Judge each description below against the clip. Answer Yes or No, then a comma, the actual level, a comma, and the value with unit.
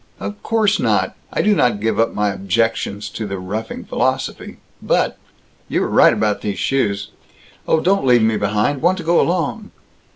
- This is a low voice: Yes, low, 110 Hz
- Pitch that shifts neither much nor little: No, wide, 8.1 semitones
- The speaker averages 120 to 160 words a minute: No, average, 175 wpm